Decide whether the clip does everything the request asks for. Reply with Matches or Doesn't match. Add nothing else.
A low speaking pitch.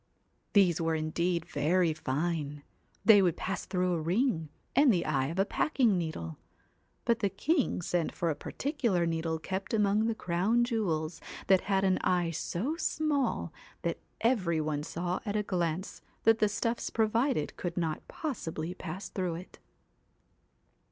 Doesn't match